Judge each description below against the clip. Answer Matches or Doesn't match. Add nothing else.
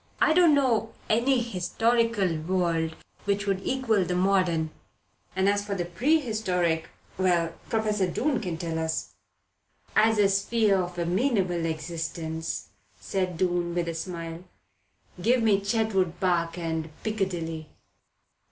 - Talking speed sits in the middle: Doesn't match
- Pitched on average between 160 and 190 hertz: Matches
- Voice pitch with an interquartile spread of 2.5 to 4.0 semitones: Doesn't match